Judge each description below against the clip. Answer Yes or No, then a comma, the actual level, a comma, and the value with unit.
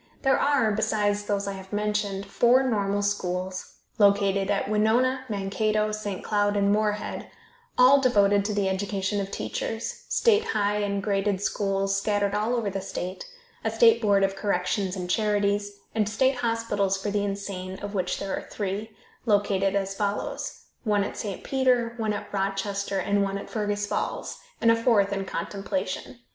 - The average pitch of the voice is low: No, high, 205 Hz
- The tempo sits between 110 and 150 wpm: No, average, 165 wpm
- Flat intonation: Yes, narrow, 1.5 semitones